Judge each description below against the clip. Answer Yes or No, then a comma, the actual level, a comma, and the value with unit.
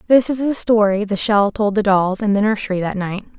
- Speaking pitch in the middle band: No, high, 210 Hz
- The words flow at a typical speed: No, fast, 250 wpm